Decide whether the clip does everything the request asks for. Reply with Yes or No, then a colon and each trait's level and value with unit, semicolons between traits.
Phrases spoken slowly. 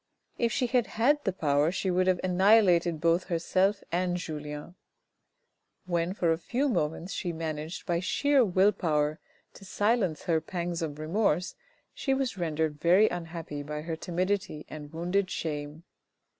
No: average, 155 wpm